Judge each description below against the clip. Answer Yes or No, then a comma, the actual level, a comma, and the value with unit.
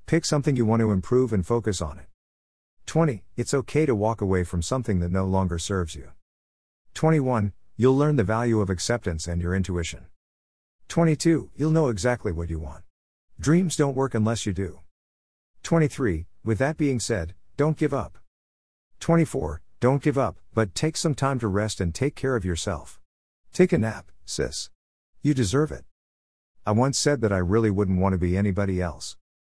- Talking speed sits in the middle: Yes, average, 180 wpm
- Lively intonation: Yes, wide, 7.9 semitones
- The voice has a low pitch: Yes, low, 100 Hz